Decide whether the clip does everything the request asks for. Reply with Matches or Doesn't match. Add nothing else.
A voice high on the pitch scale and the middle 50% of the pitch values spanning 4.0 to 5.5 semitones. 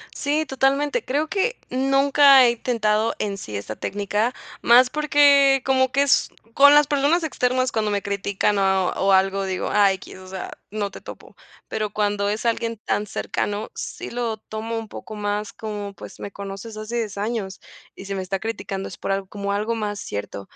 Matches